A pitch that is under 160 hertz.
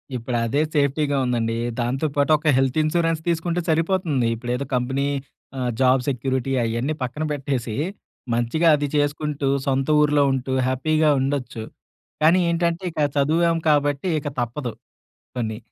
Yes: medium, 140 Hz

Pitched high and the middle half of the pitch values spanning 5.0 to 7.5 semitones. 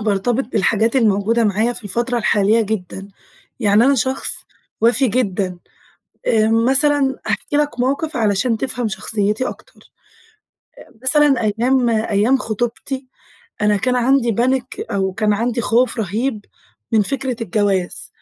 No: high, 230 Hz; average, 3.6 semitones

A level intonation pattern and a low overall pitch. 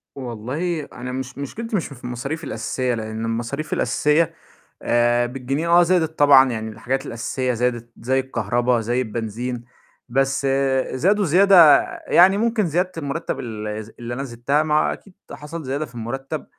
No: average, 4.6 semitones; low, 130 Hz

